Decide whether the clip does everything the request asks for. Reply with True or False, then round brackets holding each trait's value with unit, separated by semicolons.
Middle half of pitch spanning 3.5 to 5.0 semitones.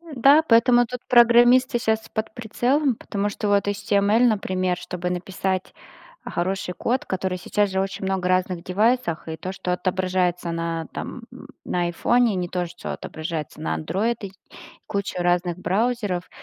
True (4.2 semitones)